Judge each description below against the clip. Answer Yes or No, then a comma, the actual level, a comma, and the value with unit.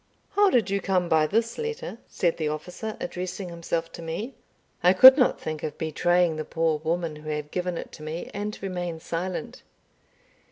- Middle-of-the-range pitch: Yes, medium, 175 Hz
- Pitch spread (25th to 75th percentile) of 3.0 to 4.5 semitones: Yes, average, 3.7 semitones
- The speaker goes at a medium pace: Yes, average, 185 wpm